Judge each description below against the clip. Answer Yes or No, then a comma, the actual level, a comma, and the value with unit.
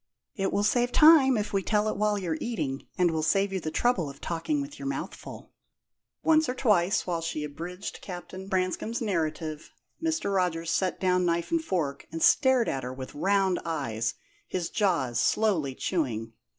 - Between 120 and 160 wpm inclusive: No, average, 180 wpm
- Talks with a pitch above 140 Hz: Yes, medium, 185 Hz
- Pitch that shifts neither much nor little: Yes, average, 5.0 semitones